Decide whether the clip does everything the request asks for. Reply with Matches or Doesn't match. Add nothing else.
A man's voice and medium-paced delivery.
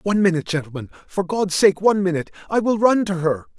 Doesn't match